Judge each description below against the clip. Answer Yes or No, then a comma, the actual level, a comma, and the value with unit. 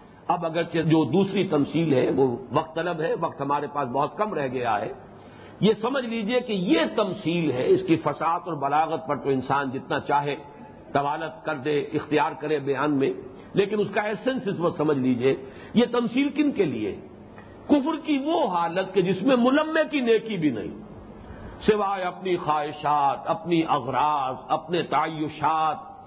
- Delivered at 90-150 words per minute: No, average, 170 wpm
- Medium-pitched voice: Yes, medium, 165 Hz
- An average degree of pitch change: No, wide, 6.3 semitones